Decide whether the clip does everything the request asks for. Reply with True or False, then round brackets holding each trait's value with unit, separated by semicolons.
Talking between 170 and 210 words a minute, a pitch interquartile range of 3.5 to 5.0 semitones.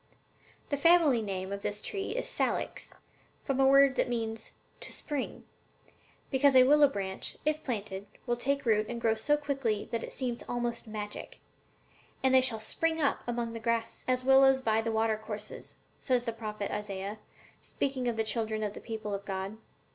True (185 wpm; 3.8 semitones)